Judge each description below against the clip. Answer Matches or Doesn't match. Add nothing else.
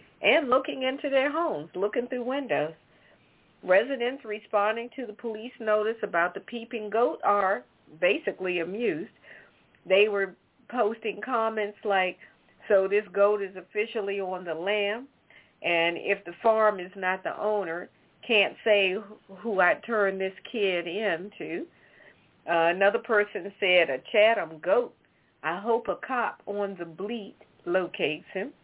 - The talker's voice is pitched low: Doesn't match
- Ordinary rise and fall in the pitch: Matches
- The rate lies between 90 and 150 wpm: Matches